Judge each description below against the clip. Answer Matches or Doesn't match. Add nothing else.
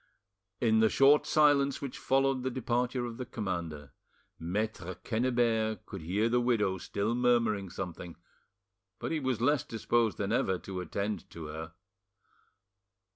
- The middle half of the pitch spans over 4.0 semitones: Matches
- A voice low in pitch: Matches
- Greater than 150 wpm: Doesn't match